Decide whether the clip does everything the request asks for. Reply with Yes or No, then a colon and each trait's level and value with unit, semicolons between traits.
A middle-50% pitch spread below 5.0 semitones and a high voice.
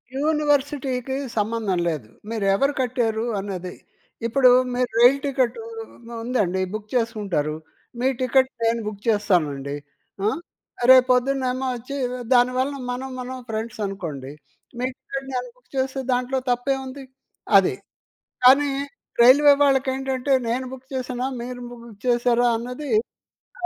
Yes: average, 3.1 semitones; very high, 250 Hz